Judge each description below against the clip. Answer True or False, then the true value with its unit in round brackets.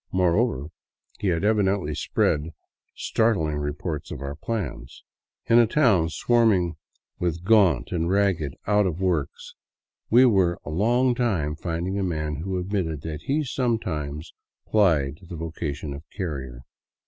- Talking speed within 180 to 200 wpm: False (140 wpm)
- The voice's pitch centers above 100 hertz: False (85 Hz)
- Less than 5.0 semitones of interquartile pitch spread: False (5.3 semitones)